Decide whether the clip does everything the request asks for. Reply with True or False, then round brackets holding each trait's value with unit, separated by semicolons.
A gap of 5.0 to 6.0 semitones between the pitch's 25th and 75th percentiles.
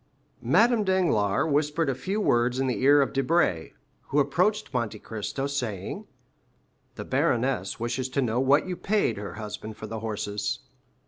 True (5.3 semitones)